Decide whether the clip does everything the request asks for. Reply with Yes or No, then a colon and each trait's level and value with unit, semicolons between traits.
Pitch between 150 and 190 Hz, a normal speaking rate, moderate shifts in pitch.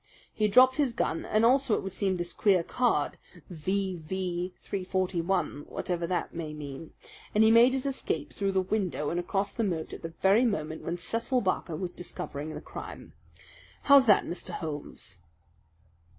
Yes: medium, 185 Hz; average, 165 wpm; average, 4.4 semitones